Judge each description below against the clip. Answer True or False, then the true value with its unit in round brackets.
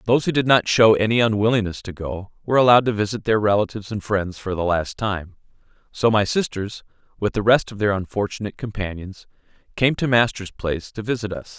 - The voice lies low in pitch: True (105 Hz)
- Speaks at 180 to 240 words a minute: True (195 wpm)